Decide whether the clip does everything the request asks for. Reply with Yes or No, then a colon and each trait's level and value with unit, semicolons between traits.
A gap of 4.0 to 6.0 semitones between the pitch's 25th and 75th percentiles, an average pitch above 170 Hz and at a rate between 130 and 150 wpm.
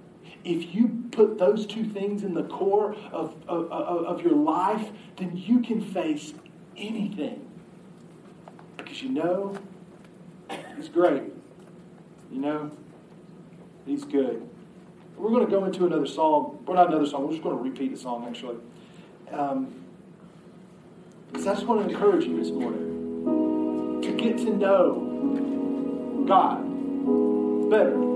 Yes: average, 5.3 semitones; medium, 185 Hz; slow, 135 wpm